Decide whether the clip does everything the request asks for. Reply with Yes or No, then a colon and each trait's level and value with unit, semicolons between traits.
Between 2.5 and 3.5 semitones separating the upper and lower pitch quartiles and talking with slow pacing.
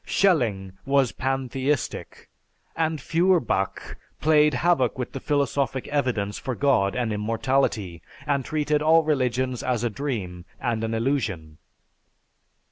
No: average, 4.6 semitones; slow, 120 wpm